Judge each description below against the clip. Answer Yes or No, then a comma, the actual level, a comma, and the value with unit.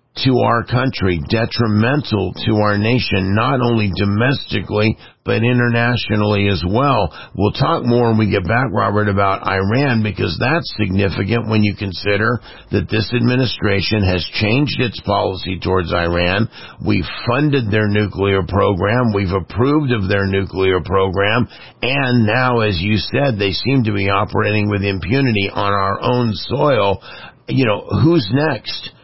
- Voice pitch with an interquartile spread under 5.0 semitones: Yes, average, 3.6 semitones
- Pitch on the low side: Yes, low, 105 Hz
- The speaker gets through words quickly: No, average, 145 wpm